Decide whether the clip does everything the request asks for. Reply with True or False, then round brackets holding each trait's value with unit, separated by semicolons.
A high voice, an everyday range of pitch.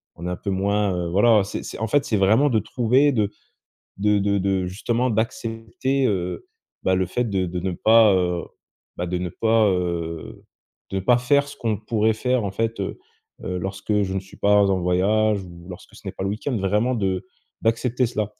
False (105 Hz; 3.3 semitones)